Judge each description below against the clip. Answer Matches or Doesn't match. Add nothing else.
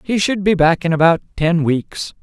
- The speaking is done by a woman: Doesn't match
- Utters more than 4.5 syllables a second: Matches